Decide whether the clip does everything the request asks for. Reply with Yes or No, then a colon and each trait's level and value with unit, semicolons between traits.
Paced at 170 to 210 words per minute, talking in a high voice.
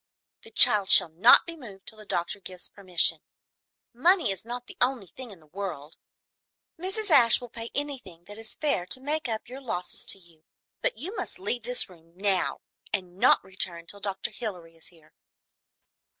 Yes: average, 185 wpm; high, 205 Hz